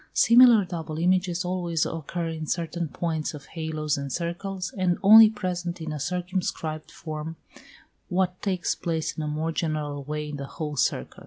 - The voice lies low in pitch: No, medium, 165 Hz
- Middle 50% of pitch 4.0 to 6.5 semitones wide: No, average, 2.8 semitones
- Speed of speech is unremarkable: Yes, average, 165 wpm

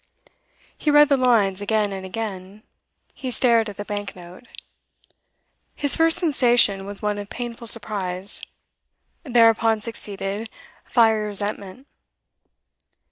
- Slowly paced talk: Yes, slow, 115 wpm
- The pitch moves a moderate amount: Yes, average, 3.0 semitones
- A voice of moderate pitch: No, high, 215 Hz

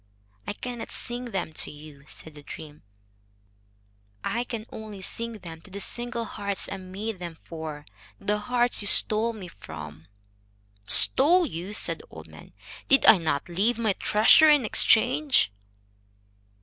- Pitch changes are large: Yes, wide, 6.2 semitones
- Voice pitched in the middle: No, high, 205 Hz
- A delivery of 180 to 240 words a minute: No, average, 150 wpm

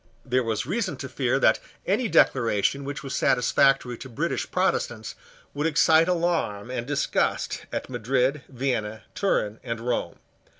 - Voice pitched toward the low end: Yes, low, 130 Hz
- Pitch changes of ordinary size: Yes, average, 4.3 semitones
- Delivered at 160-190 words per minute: No, average, 140 wpm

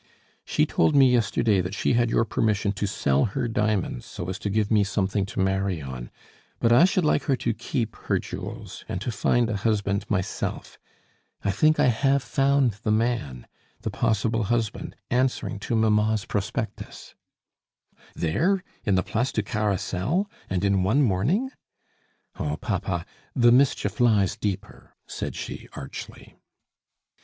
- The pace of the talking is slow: No, average, 155 wpm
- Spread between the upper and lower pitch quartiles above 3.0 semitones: Yes, average, 3.9 semitones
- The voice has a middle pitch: No, low, 110 Hz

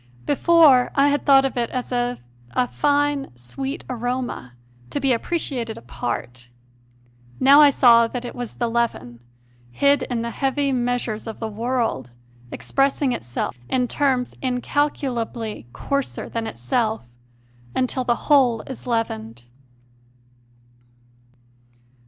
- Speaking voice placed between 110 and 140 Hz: No, high, 245 Hz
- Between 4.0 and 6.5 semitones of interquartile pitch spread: No, average, 3.3 semitones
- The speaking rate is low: Yes, slow, 130 wpm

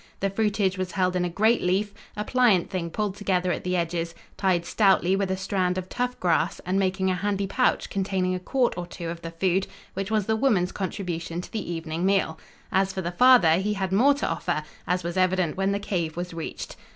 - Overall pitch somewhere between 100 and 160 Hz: No, medium, 185 Hz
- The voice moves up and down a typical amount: No, narrow, 2.3 semitones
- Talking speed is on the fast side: Yes, fast, 225 wpm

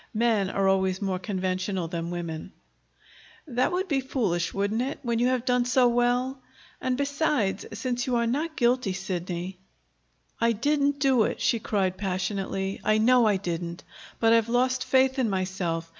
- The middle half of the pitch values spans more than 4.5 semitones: Yes, average, 5.2 semitones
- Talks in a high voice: Yes, high, 225 Hz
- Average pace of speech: Yes, average, 170 wpm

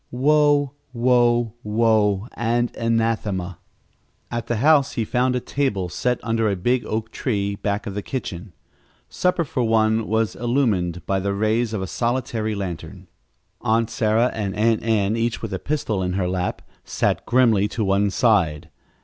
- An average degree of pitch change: Yes, average, 3.1 semitones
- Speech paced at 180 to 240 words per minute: No, average, 160 wpm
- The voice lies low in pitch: Yes, low, 110 Hz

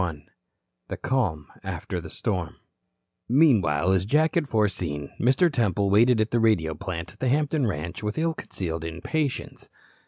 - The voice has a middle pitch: No, low, 105 Hz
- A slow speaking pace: No, average, 155 wpm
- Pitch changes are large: Yes, wide, 7.5 semitones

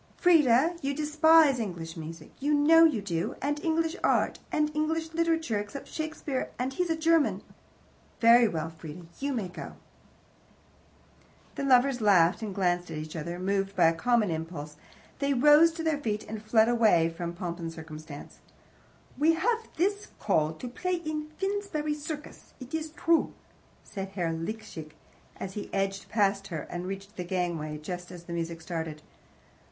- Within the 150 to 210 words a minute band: Yes, average, 160 wpm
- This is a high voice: Yes, high, 220 Hz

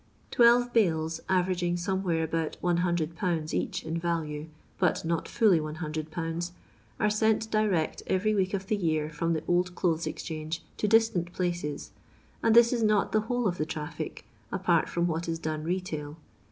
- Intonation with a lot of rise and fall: No, average, 3.4 semitones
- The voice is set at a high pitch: No, medium, 175 Hz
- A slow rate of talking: No, average, 160 wpm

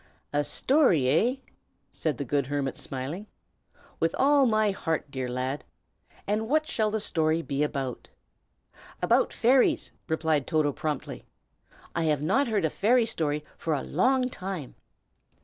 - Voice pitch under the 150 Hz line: No, medium, 160 Hz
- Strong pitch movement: Yes, wide, 7.3 semitones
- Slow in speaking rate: No, average, 145 wpm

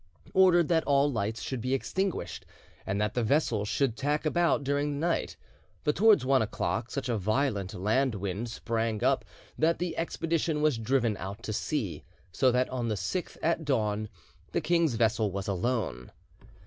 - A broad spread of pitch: Yes, wide, 5.8 semitones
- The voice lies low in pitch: Yes, low, 130 Hz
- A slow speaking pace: No, average, 175 wpm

